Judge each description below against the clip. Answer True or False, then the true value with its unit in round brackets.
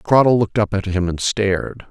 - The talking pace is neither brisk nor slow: False (220 wpm)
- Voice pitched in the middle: False (100 Hz)